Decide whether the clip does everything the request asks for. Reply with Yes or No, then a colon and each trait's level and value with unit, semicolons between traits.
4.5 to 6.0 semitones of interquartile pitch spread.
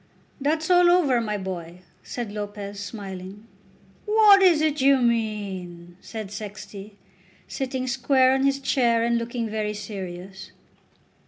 Yes: average, 5.1 semitones